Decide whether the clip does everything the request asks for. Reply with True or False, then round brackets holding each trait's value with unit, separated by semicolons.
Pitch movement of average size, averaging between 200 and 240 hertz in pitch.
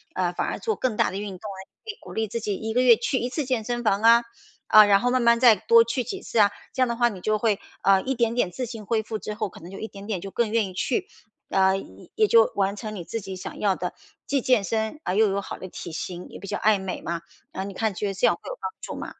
True (3.4 semitones; 215 Hz)